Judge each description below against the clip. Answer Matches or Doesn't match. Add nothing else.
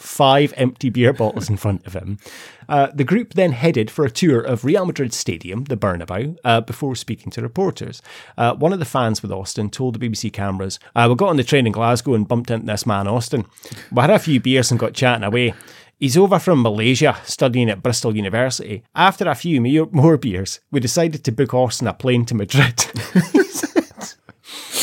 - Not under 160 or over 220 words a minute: Matches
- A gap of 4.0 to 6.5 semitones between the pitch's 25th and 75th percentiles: Matches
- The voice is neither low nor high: Doesn't match